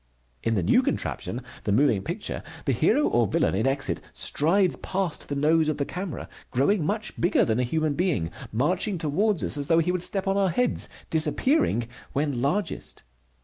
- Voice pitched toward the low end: No, medium, 155 Hz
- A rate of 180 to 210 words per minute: Yes, average, 185 wpm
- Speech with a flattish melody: No, wide, 5.6 semitones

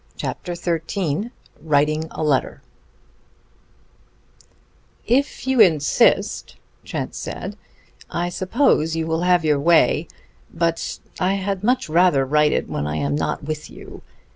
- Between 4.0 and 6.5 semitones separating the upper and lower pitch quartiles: No, average, 3.4 semitones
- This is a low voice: No, medium, 165 Hz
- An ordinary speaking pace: No, slow, 125 wpm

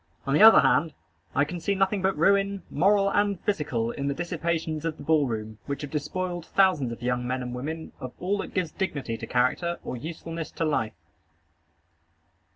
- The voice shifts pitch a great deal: Yes, wide, 5.7 semitones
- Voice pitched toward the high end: No, medium, 160 Hz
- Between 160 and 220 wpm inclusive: Yes, average, 190 wpm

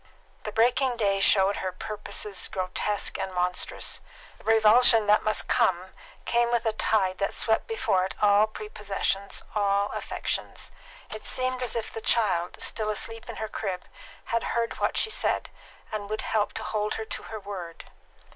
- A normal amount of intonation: No, narrow, 2.3 semitones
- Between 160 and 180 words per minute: Yes, average, 165 wpm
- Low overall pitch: No, high, 210 Hz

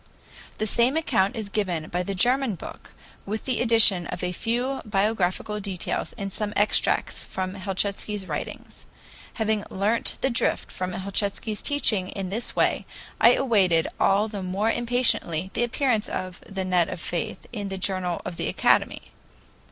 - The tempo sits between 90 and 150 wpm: No, average, 160 wpm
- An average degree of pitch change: Yes, average, 3.4 semitones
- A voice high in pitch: Yes, high, 200 Hz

